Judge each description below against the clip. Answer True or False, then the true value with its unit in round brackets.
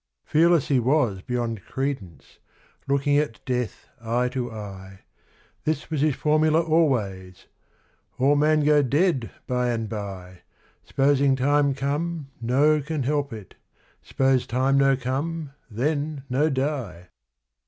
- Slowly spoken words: True (125 wpm)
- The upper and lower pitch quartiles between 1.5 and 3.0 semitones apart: False (4.1 semitones)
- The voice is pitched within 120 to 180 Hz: True (135 Hz)